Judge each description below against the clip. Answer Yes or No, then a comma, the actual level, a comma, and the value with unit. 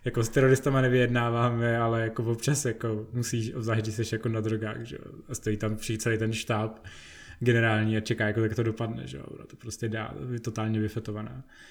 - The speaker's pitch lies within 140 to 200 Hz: No, low, 115 Hz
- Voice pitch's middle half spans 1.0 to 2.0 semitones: Yes, narrow, 1.7 semitones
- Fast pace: Yes, fast, 190 wpm